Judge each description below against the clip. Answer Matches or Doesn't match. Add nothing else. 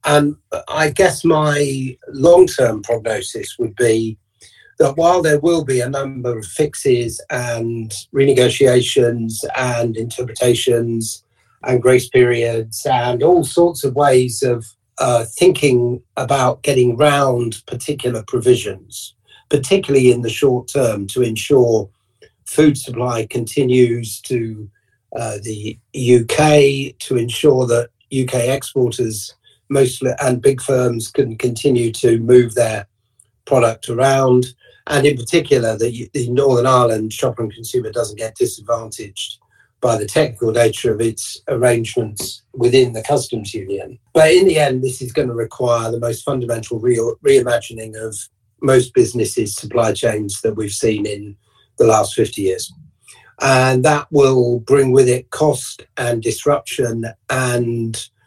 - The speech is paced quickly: Doesn't match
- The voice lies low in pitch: Matches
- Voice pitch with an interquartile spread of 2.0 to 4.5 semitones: Matches